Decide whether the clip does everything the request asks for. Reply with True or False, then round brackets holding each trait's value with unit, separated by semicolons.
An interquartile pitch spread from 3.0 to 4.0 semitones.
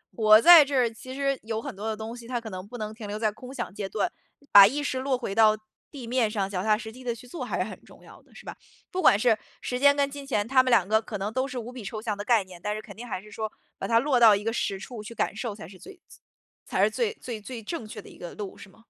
True (3.4 semitones)